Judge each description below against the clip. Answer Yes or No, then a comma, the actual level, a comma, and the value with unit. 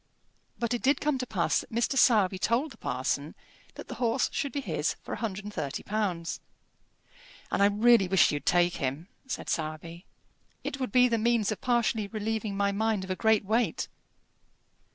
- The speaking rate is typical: Yes, average, 175 wpm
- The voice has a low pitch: No, high, 215 Hz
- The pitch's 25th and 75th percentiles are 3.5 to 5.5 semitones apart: Yes, average, 4.2 semitones